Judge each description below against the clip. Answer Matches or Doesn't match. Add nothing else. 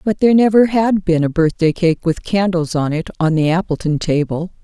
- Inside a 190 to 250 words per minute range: Matches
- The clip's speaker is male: Doesn't match